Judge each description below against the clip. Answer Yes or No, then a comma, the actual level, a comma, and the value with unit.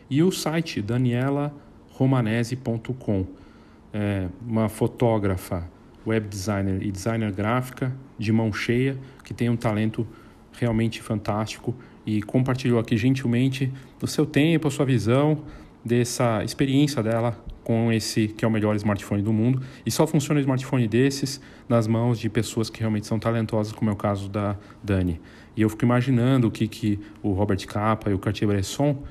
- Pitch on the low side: Yes, low, 115 Hz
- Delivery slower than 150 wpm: No, average, 160 wpm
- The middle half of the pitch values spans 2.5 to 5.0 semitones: Yes, average, 3.3 semitones